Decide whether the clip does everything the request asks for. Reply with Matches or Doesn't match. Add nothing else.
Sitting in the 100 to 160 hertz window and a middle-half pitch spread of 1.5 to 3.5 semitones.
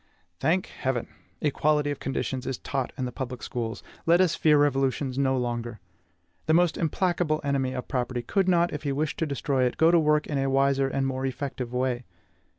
Matches